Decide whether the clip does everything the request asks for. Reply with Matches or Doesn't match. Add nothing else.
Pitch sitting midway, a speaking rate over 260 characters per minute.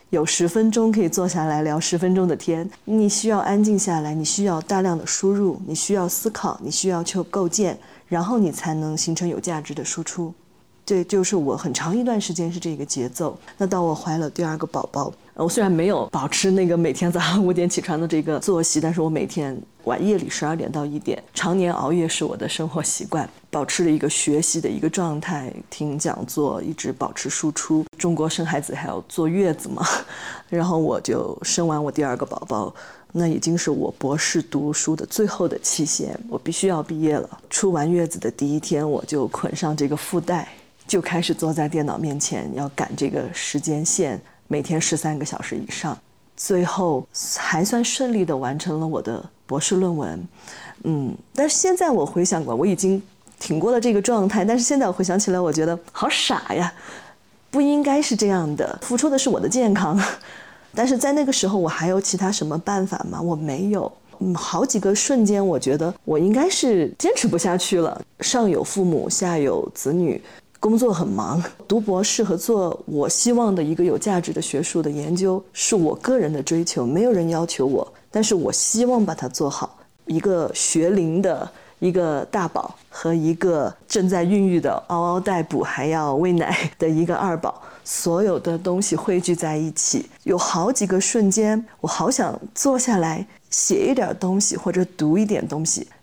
Matches